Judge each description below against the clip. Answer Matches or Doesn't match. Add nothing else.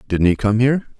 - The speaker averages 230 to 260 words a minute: Matches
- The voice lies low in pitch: Matches